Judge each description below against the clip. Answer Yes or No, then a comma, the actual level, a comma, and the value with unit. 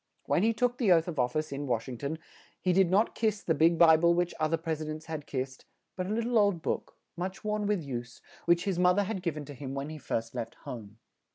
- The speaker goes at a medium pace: No, fast, 275 wpm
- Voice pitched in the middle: Yes, medium, 165 Hz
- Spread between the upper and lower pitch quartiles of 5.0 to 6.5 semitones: Yes, average, 5.3 semitones